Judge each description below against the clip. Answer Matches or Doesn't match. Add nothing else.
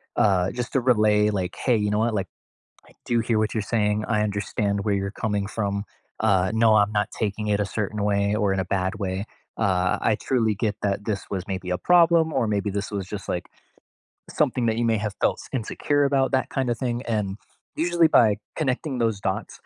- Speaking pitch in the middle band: Doesn't match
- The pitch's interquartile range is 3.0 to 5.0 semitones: Doesn't match